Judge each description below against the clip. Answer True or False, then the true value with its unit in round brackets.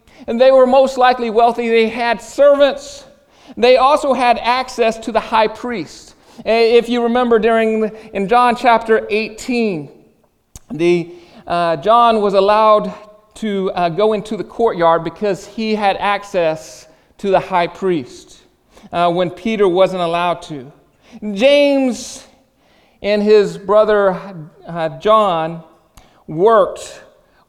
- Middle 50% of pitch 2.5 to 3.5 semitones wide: False (4.3 semitones)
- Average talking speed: False (125 wpm)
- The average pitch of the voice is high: True (215 Hz)